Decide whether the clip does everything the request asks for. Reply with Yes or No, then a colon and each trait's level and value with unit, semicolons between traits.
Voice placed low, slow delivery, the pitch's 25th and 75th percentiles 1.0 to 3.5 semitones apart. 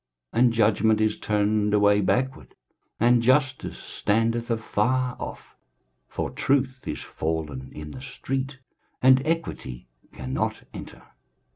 No: low, 115 Hz; slow, 120 wpm; average, 4.1 semitones